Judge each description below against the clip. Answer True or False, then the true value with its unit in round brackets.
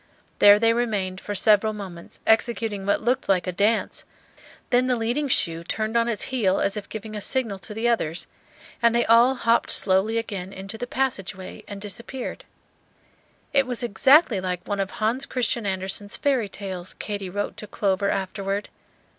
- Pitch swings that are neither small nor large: True (3.3 semitones)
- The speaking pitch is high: True (210 Hz)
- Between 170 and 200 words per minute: True (175 wpm)